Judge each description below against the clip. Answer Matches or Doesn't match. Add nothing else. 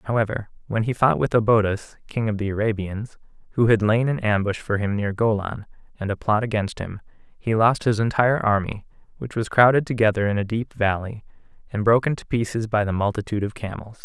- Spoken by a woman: Doesn't match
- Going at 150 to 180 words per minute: Doesn't match